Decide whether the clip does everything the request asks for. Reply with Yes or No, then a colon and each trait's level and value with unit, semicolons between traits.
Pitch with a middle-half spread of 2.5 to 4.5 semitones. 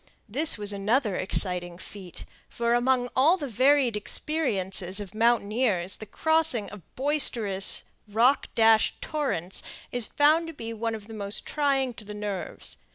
No: average, 5.0 semitones